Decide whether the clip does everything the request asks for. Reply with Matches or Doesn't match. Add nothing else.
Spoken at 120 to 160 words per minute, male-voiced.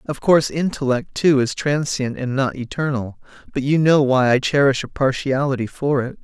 Doesn't match